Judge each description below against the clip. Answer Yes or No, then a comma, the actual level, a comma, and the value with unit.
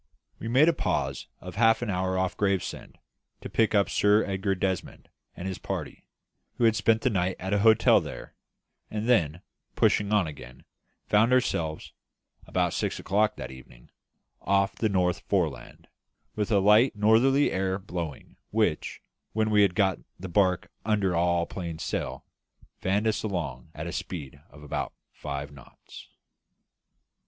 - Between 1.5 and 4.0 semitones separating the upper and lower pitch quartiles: Yes, average, 3.6 semitones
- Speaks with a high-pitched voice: No, very low, 95 Hz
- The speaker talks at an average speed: Yes, average, 155 wpm